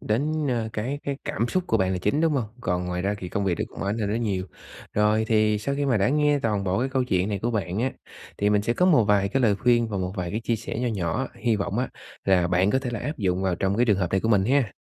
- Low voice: Yes, low, 105 Hz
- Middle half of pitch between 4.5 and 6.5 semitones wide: No, average, 4.1 semitones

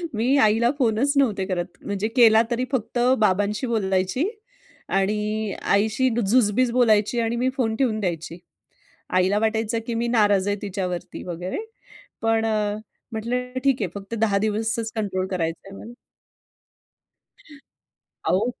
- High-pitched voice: Yes, high, 215 Hz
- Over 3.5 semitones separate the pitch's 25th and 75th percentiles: No, average, 3.0 semitones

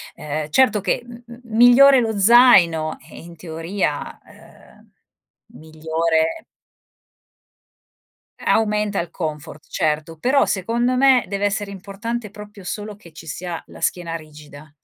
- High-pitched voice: Yes, high, 195 Hz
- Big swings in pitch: Yes, wide, 6.1 semitones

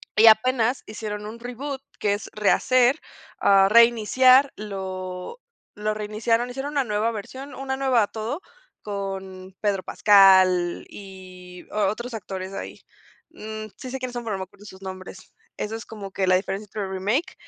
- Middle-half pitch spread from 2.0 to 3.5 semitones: No, average, 3.9 semitones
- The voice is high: Yes, high, 210 Hz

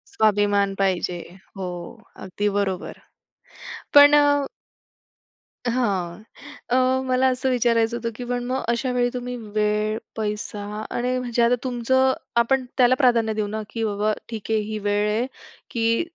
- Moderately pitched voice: No, high, 230 Hz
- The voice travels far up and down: No, average, 2.9 semitones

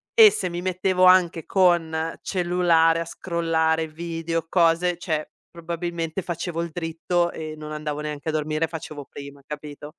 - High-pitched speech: No, medium, 165 Hz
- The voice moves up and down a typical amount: No, narrow, 1.9 semitones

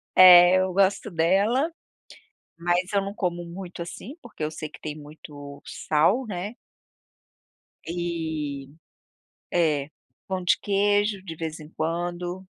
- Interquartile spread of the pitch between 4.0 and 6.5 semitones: No, average, 3.5 semitones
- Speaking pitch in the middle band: Yes, medium, 175 Hz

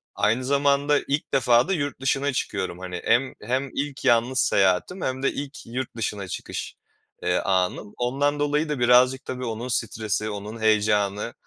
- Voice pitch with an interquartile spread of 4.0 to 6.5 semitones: Yes, average, 4.5 semitones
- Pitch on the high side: No, low, 125 Hz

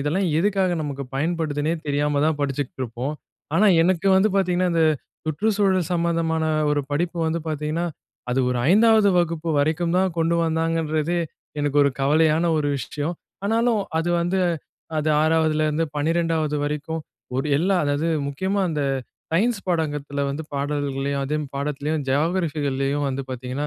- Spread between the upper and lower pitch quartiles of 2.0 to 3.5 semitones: Yes, average, 3.1 semitones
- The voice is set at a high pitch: No, medium, 155 Hz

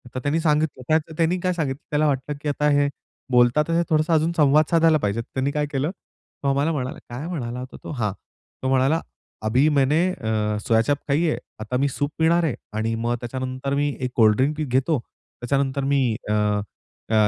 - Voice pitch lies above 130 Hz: Yes, medium, 140 Hz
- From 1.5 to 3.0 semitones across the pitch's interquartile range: No, average, 3.5 semitones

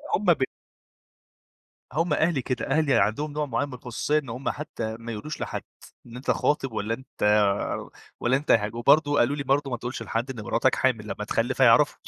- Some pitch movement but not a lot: Yes, average, 3.9 semitones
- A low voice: Yes, low, 130 Hz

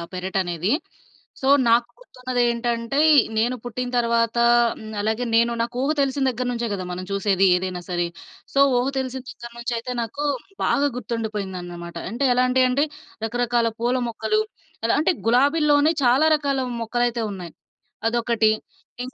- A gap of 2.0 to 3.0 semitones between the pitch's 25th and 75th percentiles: Yes, average, 2.7 semitones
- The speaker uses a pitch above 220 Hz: Yes, high, 235 Hz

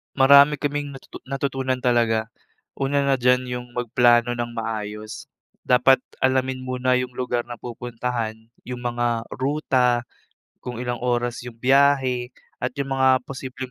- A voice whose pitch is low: Yes, low, 125 Hz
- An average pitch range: No, narrow, 1.6 semitones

